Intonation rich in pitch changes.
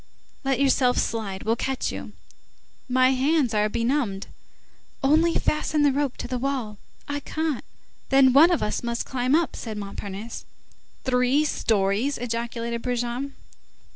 No: average, 3.3 semitones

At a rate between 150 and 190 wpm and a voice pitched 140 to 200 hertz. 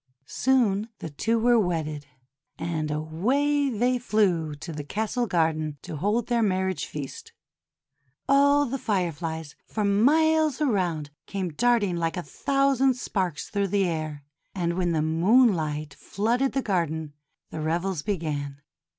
No: slow, 135 wpm; high, 190 Hz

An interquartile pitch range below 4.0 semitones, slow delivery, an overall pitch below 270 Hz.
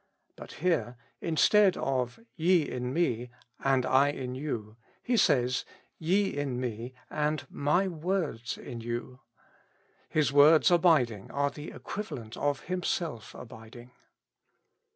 No: average, 5.2 semitones; slow, 115 wpm; medium, 140 Hz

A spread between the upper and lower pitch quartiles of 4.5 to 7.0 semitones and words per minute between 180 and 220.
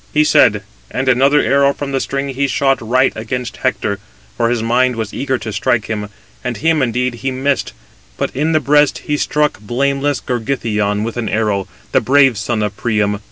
No: average, 3.7 semitones; average, 190 wpm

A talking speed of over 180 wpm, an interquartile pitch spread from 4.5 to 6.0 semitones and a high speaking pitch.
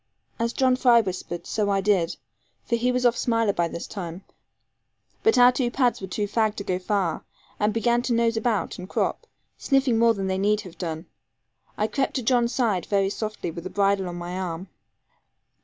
No: average, 200 wpm; average, 4.1 semitones; high, 210 Hz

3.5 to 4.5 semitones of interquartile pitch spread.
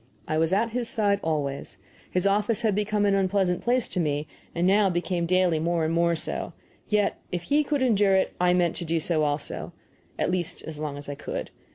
Yes: average, 4.0 semitones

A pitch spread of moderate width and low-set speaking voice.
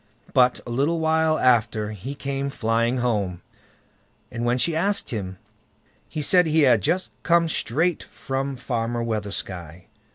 No: wide, 5.8 semitones; low, 125 Hz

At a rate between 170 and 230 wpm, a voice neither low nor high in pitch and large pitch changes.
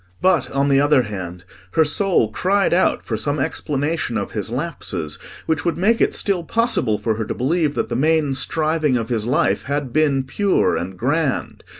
Yes: average, 190 wpm; medium, 145 Hz; wide, 5.8 semitones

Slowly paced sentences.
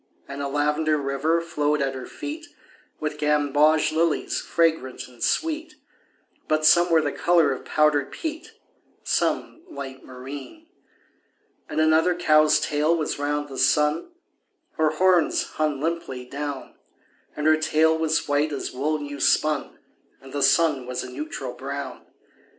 No: average, 145 wpm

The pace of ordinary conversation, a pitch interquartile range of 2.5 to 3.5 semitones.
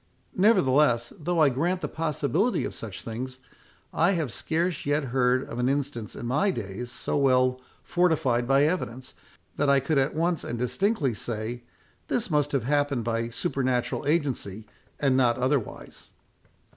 No: average, 155 wpm; average, 4.2 semitones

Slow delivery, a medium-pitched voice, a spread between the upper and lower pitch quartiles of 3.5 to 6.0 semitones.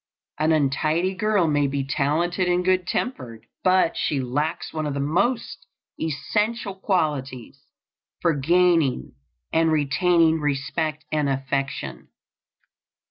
Yes: slow, 115 wpm; medium, 155 Hz; average, 4.3 semitones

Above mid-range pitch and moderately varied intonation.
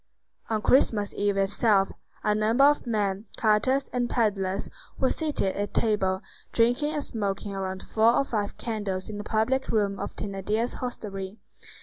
Yes: high, 210 Hz; average, 3.1 semitones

